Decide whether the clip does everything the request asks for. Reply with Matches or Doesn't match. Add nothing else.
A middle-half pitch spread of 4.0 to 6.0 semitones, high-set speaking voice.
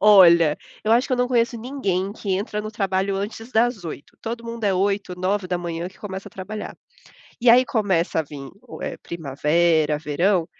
Matches